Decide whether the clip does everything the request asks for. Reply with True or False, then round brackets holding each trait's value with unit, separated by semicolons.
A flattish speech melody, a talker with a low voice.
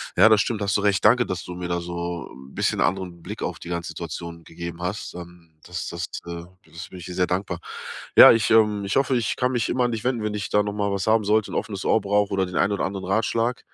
False (3.6 semitones; 95 Hz)